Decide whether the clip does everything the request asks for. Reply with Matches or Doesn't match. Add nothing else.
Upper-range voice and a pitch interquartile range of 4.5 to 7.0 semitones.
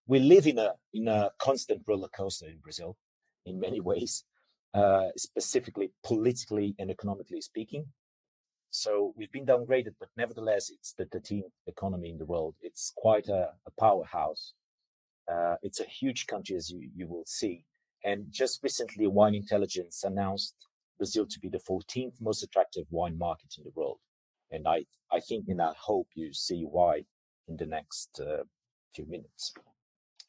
Doesn't match